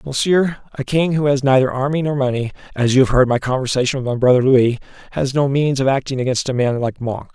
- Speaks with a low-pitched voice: Yes, low, 130 Hz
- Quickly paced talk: Yes, fast, 235 wpm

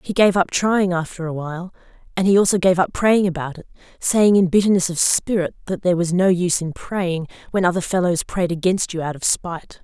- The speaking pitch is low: No, medium, 180 Hz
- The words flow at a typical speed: No, fast, 215 wpm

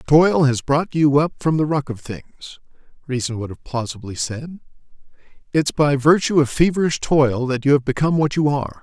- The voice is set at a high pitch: No, medium, 140 Hz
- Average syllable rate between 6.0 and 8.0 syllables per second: No, 5.4 syllables/s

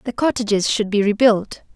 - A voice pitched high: Yes, high, 215 Hz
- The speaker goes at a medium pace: Yes, average, 170 wpm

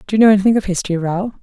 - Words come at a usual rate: No, fast, 295 wpm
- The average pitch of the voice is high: Yes, high, 195 Hz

